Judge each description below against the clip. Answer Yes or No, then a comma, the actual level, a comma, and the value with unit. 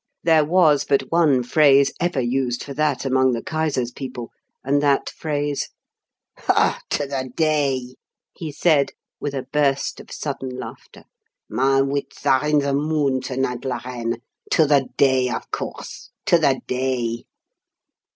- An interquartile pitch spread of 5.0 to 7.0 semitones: No, narrow, 2.4 semitones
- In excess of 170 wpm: No, average, 150 wpm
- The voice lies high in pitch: No, low, 135 Hz